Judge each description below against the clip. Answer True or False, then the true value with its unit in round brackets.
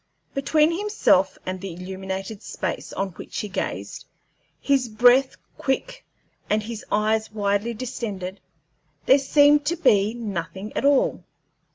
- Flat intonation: False (5.5 semitones)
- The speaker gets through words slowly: True (130 wpm)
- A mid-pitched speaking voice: False (215 Hz)